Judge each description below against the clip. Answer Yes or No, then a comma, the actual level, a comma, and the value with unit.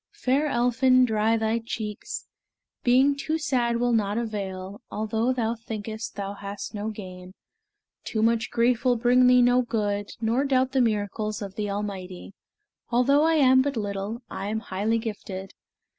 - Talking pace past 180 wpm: No, average, 160 wpm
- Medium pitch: No, high, 225 Hz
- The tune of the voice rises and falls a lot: No, average, 3.3 semitones